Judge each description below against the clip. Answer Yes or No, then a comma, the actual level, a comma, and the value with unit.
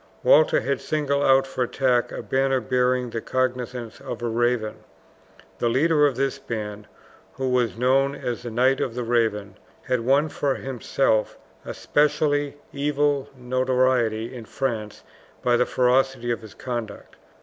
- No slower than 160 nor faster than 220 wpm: No, average, 150 wpm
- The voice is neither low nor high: No, low, 125 Hz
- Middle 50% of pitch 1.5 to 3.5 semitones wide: Yes, narrow, 2.4 semitones